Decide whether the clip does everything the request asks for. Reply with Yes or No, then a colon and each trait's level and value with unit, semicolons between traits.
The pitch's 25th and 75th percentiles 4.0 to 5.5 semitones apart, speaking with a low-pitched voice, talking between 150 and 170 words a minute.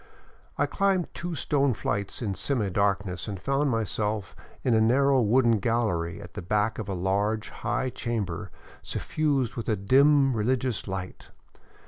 Yes: average, 4.7 semitones; low, 115 Hz; average, 160 wpm